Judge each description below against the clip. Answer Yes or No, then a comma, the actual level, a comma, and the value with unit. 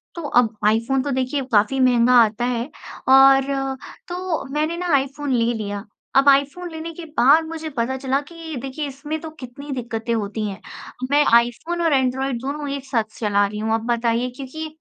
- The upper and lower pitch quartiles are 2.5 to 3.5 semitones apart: No, average, 3.9 semitones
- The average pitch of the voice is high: Yes, very high, 265 Hz